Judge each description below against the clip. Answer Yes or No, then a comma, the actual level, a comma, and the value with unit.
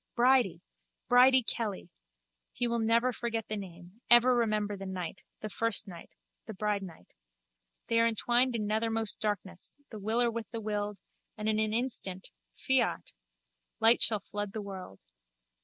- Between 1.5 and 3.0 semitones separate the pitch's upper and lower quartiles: Yes, narrow, 2.6 semitones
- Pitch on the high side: Yes, high, 220 Hz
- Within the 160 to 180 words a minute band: No, average, 145 wpm